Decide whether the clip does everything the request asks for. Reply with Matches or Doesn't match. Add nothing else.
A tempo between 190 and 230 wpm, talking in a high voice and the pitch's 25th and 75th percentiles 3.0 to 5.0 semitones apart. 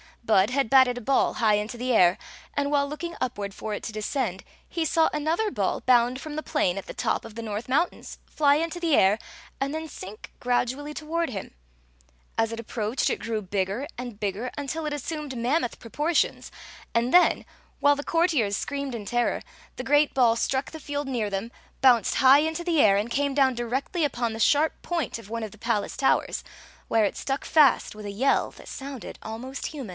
Matches